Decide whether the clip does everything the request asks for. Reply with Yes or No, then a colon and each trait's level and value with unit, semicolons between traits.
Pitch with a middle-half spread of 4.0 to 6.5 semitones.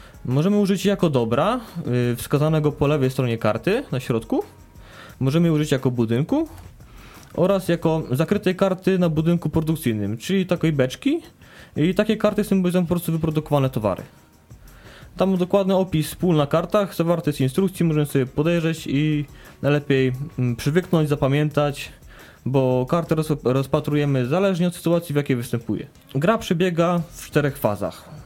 Yes: average, 4.8 semitones